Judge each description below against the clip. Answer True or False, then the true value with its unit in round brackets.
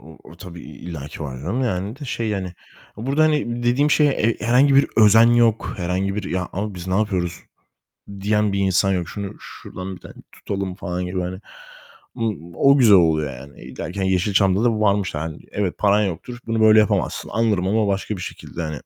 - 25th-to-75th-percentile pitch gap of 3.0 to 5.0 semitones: True (3.9 semitones)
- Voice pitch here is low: True (100 Hz)